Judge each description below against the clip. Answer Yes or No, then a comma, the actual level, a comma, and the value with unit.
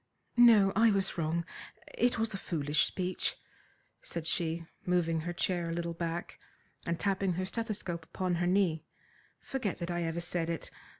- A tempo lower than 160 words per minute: No, average, 165 wpm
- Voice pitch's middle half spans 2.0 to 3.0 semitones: Yes, narrow, 2.6 semitones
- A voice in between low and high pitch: Yes, medium, 175 Hz